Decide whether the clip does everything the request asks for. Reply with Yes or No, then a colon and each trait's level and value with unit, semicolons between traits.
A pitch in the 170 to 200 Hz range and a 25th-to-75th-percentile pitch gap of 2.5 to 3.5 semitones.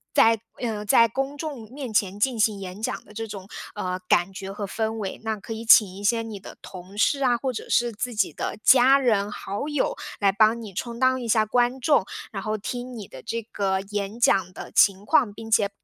No: high, 220 Hz; average, 3.2 semitones